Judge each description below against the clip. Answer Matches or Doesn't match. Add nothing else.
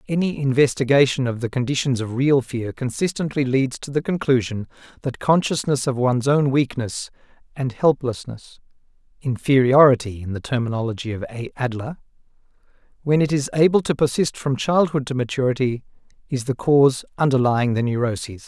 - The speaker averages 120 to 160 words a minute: Matches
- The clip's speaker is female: Doesn't match